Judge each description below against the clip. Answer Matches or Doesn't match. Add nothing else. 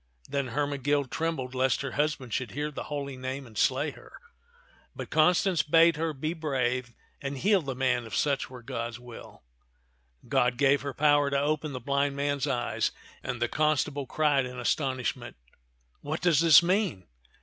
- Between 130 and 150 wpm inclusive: Doesn't match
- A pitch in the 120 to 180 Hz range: Matches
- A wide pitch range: Doesn't match